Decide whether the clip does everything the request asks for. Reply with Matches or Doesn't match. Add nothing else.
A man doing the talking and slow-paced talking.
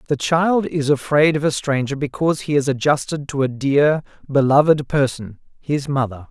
Doesn't match